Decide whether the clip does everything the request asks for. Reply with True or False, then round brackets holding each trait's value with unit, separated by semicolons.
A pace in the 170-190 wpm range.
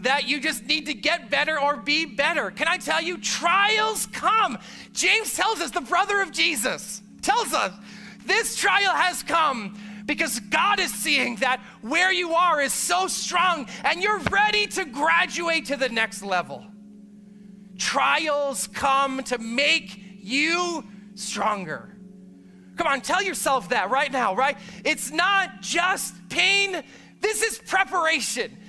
False (145 wpm)